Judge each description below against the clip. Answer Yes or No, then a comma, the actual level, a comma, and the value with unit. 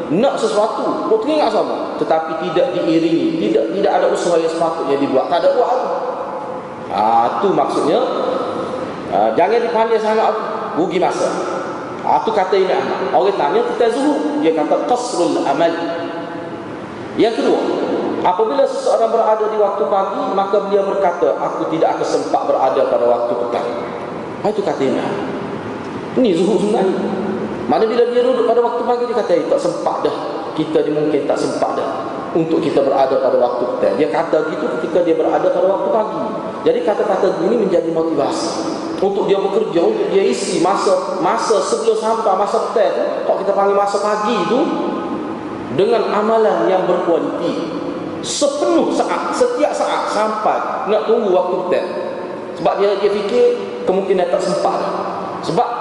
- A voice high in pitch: Yes, high, 195 Hz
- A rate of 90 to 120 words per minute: No, fast, 155 wpm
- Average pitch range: No, wide, 6.0 semitones